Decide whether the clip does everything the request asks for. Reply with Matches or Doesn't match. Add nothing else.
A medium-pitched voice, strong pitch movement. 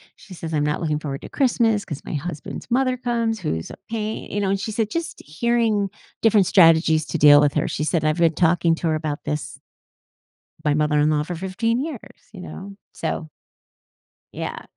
Matches